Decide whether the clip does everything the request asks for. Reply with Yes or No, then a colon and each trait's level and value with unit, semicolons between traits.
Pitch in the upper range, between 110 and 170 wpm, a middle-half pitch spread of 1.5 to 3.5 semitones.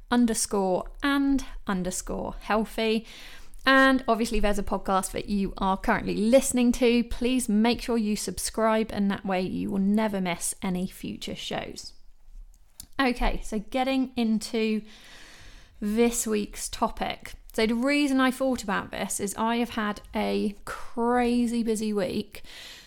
Yes: high, 225 Hz; slow, 135 wpm; average, 2.9 semitones